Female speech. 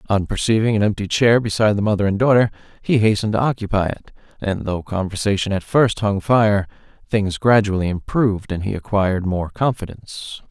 No: male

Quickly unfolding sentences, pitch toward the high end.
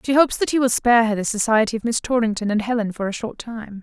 Yes: fast, 285 wpm; high, 225 Hz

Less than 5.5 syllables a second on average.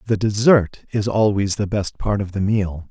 Yes: 4.5 syllables/s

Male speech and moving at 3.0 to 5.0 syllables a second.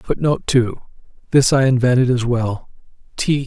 Yes: male; 4.9 syllables/s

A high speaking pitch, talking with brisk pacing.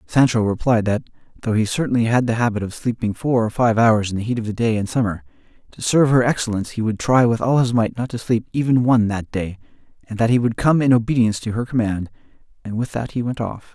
No: low, 115 Hz; fast, 250 wpm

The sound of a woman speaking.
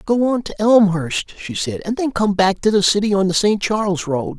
No: male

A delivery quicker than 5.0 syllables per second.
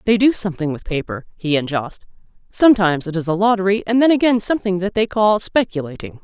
Yes: 6.3 syllables/s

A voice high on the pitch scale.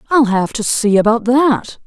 Yes: high, 235 Hz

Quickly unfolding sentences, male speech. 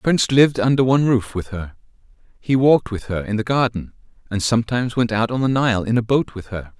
Yes: fast, 240 wpm; male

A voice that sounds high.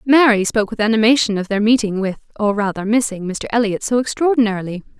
Yes: high, 220 Hz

